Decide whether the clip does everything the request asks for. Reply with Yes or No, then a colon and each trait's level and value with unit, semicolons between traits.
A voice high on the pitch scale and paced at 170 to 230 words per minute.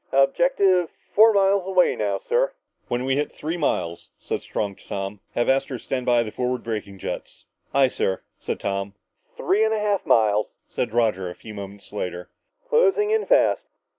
No: low, 125 Hz; average, 175 wpm